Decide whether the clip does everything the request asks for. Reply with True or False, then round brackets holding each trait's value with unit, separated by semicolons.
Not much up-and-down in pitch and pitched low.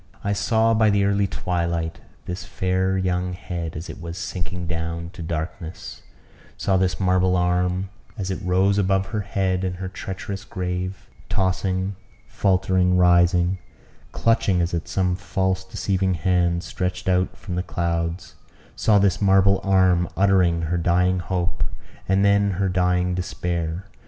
True (1.5 semitones; 90 Hz)